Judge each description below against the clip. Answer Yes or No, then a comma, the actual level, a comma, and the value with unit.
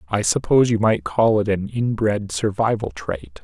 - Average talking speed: Yes, average, 175 wpm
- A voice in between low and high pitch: No, low, 100 Hz